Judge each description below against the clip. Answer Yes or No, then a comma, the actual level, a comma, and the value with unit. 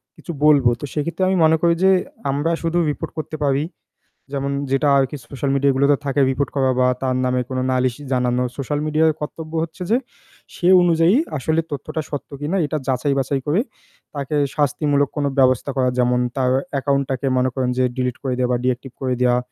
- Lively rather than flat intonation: No, average, 3.0 semitones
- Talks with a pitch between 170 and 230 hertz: No, medium, 140 Hz